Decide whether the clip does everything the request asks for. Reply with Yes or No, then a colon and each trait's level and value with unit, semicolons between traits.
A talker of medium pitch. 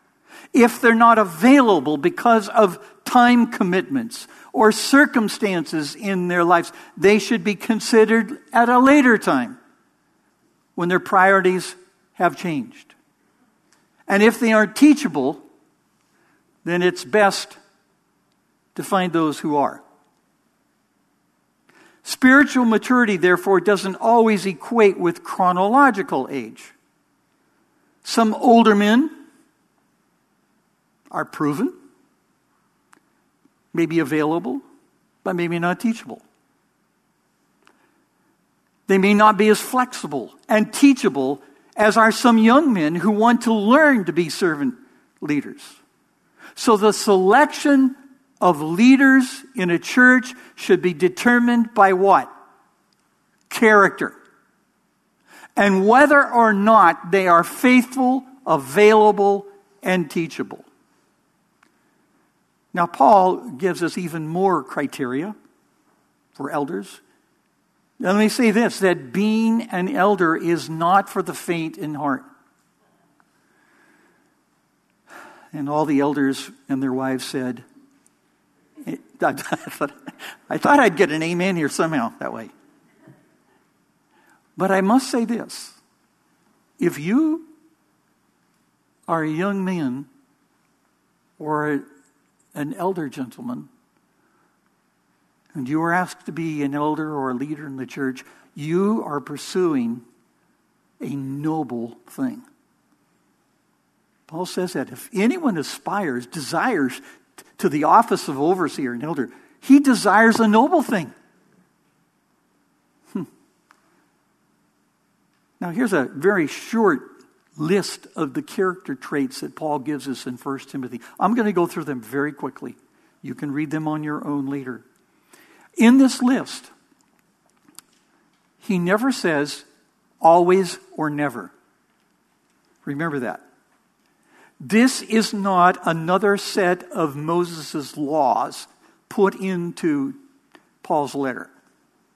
No: high, 200 Hz